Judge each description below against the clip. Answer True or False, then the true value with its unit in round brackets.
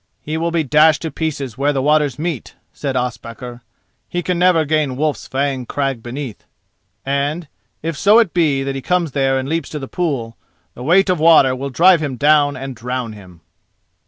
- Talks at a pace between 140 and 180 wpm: False (190 wpm)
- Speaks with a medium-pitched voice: True (145 Hz)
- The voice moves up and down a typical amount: True (3.7 semitones)